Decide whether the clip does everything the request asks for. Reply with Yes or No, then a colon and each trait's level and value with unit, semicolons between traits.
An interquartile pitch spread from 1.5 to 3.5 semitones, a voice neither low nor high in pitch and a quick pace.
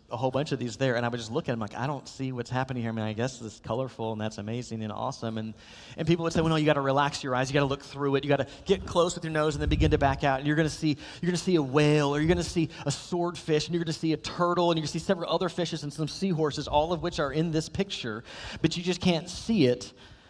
No: average, 4.5 semitones; medium, 145 Hz; fast, 335 wpm